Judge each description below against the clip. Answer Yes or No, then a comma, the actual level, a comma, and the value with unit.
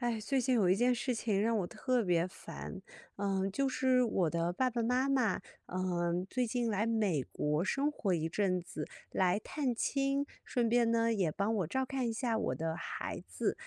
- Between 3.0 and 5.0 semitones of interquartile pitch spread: No, wide, 5.4 semitones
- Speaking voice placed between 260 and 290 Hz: No, high, 220 Hz